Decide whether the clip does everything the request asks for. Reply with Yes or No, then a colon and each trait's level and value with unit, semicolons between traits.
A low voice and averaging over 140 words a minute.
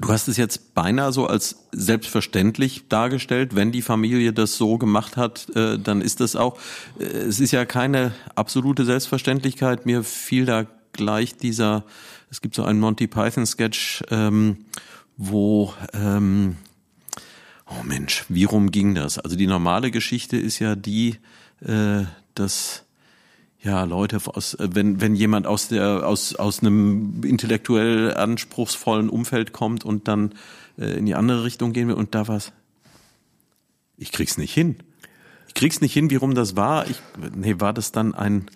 Yes: low, 110 Hz; average, 150 wpm